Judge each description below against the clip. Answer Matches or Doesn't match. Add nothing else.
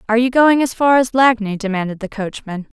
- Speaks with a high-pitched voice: Matches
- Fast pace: Matches